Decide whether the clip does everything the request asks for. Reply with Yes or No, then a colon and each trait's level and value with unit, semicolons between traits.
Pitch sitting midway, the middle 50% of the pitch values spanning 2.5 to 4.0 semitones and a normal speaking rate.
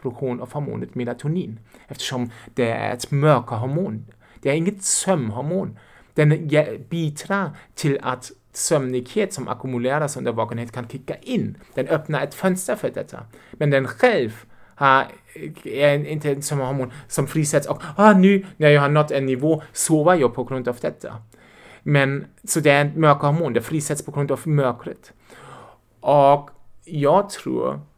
Yes: medium, 145 Hz; average, 3.5 semitones; average, 150 wpm